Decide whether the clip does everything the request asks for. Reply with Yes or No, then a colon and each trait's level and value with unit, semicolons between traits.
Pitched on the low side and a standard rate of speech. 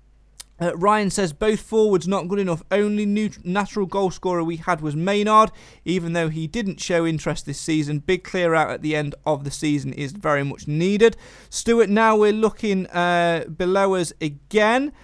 No: medium, 180 Hz; average, 185 wpm